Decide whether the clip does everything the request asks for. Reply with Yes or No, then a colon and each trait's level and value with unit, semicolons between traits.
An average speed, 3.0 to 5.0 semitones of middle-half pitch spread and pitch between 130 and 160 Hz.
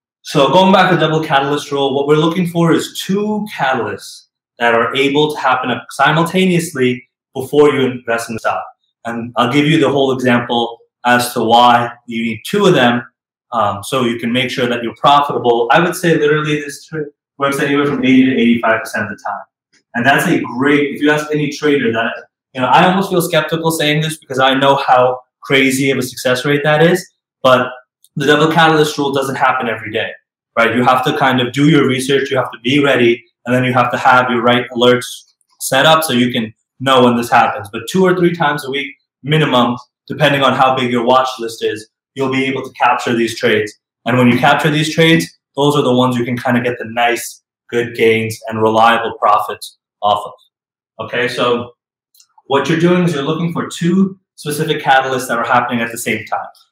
No: fast, 215 wpm; average, 3.8 semitones; low, 135 Hz